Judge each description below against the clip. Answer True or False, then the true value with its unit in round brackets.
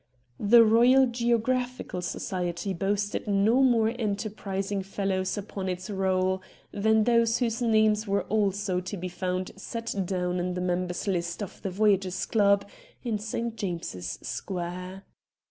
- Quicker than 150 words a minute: False (135 wpm)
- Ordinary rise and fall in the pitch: True (3.2 semitones)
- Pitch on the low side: False (200 Hz)